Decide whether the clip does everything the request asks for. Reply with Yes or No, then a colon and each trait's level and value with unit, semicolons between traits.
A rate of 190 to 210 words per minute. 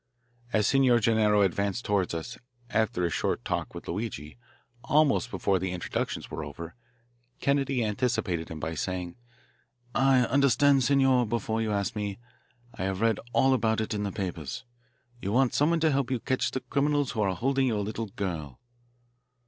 No: average, 165 wpm